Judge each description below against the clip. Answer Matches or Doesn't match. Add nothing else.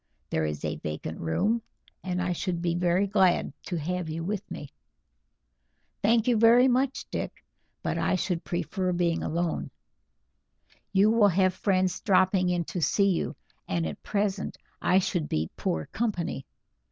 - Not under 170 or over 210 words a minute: Doesn't match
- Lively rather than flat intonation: Doesn't match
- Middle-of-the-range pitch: Matches